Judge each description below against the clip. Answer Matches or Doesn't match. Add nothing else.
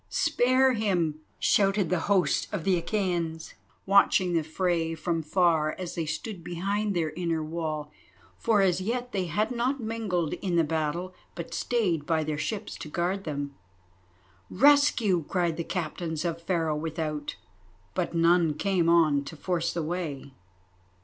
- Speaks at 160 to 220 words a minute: Doesn't match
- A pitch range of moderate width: Matches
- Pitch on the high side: Doesn't match